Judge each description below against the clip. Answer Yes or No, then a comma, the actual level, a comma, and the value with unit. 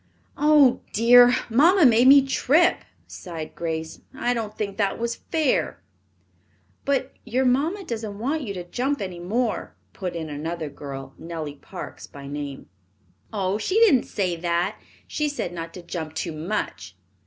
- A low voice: No, high, 210 Hz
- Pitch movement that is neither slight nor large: No, wide, 7.7 semitones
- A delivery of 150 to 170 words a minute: Yes, average, 155 wpm